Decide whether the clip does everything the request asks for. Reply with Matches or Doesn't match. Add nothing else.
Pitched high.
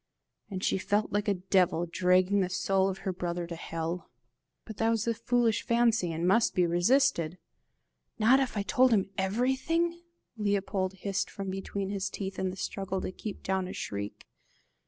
Matches